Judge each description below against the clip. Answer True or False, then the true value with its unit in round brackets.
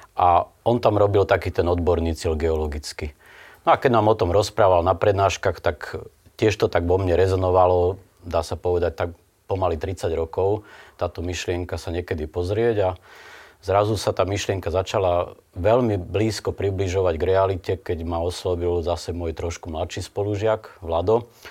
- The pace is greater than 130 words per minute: True (160 wpm)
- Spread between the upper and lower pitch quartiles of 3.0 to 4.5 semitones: False (2.4 semitones)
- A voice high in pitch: False (90 Hz)